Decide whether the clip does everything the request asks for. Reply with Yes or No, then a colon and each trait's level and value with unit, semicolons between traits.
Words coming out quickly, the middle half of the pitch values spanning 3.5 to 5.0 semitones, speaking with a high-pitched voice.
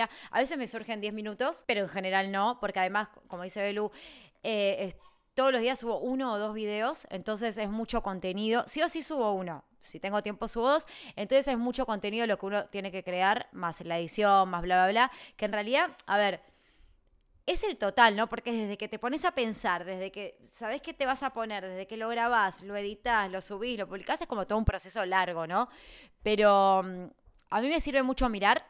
Yes: fast, 215 wpm; average, 3.9 semitones; high, 215 Hz